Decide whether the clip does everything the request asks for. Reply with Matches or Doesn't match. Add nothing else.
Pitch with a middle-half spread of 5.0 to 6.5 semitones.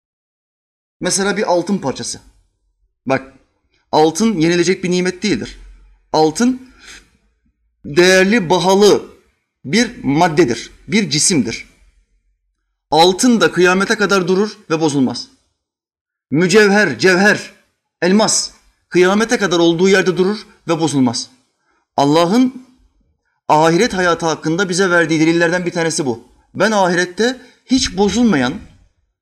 Matches